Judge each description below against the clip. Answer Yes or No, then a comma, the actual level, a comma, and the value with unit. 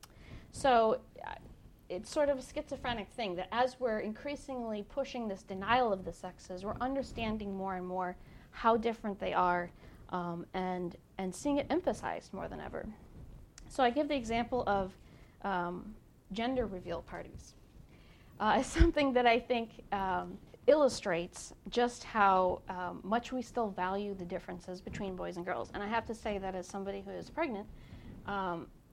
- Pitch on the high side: Yes, high, 205 Hz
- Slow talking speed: No, average, 165 wpm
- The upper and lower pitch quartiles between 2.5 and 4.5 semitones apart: No, average, 4.9 semitones